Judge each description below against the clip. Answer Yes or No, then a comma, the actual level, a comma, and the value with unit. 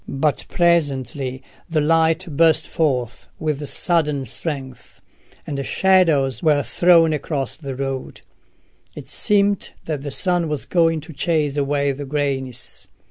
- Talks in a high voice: No, medium, 150 Hz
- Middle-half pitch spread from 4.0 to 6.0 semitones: No, average, 3.2 semitones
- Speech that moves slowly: Yes, slow, 130 wpm